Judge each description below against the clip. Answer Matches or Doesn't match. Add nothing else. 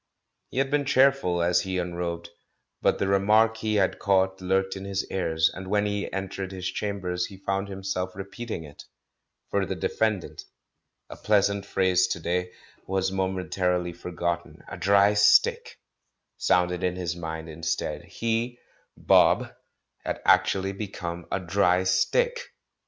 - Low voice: Matches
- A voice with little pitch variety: Matches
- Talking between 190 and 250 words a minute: Doesn't match